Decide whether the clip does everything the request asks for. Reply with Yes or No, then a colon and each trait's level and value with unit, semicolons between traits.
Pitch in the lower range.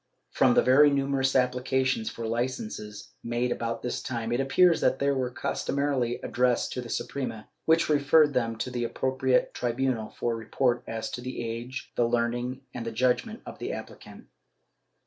Yes: low, 125 Hz